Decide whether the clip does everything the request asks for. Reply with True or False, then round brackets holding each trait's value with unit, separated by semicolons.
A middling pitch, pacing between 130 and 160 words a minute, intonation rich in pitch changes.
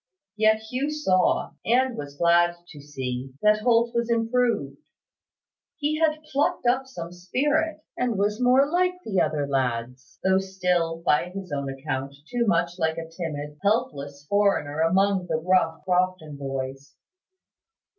True (180 Hz; 140 wpm; 8.2 semitones)